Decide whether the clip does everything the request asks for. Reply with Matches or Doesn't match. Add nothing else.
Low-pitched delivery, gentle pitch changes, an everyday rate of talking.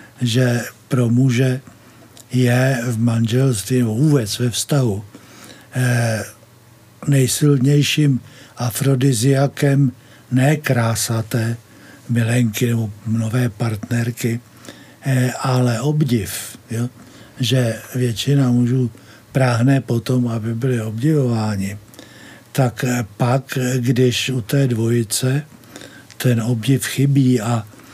Doesn't match